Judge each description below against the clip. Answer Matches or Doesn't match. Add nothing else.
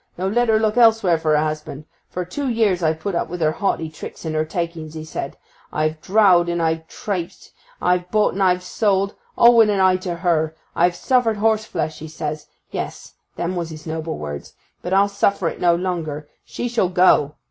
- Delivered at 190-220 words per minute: Matches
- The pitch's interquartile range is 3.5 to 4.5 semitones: Matches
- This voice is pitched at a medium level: Matches